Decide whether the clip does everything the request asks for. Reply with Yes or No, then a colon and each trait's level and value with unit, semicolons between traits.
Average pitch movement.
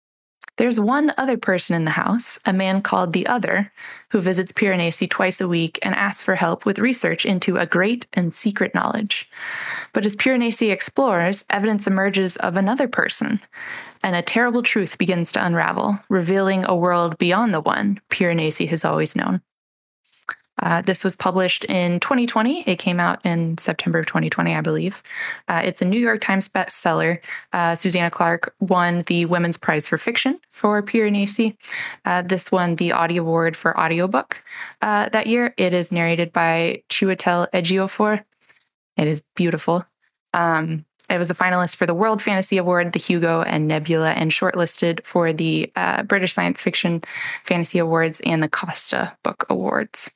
Yes: average, 3.6 semitones